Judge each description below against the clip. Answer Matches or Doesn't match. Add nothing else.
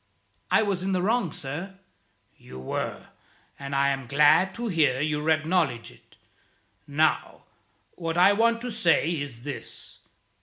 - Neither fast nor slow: Matches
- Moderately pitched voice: Matches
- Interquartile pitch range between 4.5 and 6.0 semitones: Matches